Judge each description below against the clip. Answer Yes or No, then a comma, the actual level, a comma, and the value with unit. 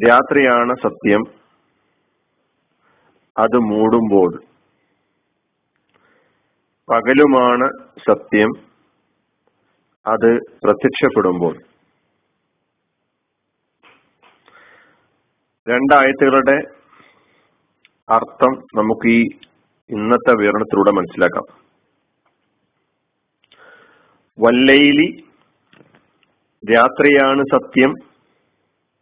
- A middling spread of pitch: Yes, average, 3.2 semitones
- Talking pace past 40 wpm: No, slow, 35 wpm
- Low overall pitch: Yes, low, 125 Hz